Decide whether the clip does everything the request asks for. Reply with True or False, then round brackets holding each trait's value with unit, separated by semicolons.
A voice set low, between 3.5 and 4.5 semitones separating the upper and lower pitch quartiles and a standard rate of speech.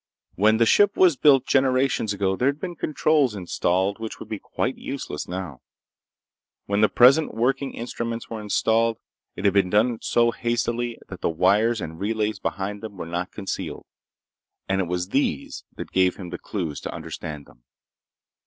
True (110 Hz; 4.2 semitones; 170 wpm)